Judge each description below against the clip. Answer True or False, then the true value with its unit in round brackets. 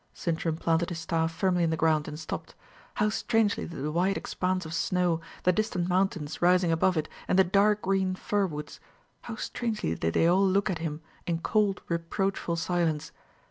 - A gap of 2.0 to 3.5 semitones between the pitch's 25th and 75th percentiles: True (2.9 semitones)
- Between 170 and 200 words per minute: True (185 wpm)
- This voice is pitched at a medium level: True (175 Hz)